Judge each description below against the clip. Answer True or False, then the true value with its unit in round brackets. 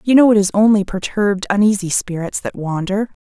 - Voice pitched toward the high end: True (200 Hz)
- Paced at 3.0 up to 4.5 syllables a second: False (5.7 syllables/s)